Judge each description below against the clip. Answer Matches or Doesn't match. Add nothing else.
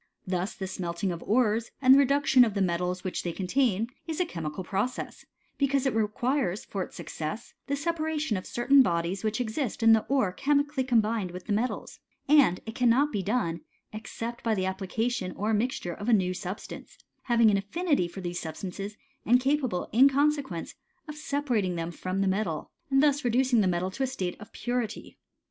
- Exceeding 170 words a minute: Matches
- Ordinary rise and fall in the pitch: Doesn't match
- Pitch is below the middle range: Doesn't match